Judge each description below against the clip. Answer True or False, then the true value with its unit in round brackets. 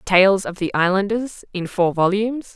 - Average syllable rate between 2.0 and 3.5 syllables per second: False (4.6 syllables/s)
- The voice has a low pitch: False (195 Hz)